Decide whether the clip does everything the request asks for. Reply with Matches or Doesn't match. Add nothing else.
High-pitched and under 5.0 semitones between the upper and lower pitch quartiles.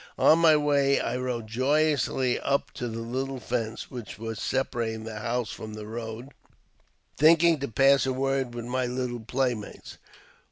Doesn't match